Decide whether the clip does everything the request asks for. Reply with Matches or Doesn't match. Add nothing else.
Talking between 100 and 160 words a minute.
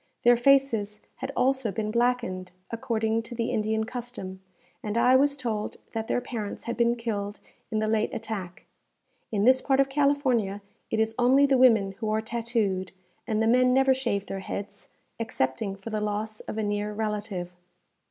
Doesn't match